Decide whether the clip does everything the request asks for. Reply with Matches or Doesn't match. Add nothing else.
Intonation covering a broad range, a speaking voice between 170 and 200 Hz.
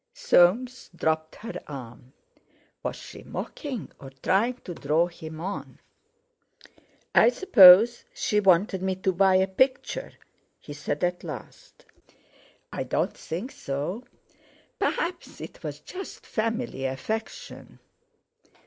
Matches